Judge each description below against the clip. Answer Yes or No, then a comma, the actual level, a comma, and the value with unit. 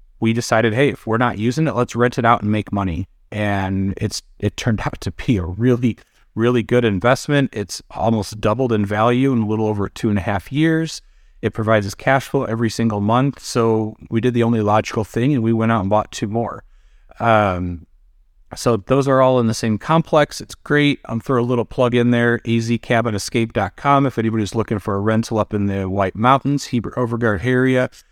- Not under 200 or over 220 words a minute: Yes, fast, 205 wpm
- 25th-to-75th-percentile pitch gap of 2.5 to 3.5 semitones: Yes, average, 3.0 semitones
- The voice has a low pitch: Yes, low, 115 Hz